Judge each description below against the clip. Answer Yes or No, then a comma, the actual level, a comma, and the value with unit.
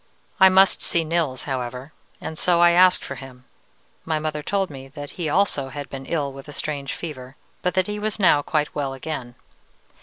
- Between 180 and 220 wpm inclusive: Yes, average, 200 wpm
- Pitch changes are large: No, average, 4.3 semitones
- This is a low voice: No, medium, 150 Hz